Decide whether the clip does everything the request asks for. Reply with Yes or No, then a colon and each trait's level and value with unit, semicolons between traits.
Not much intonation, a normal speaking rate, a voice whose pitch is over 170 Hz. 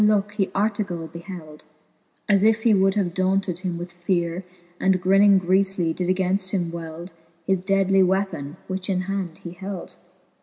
Yes: narrow, 2.0 semitones; average, 160 wpm; medium, 185 Hz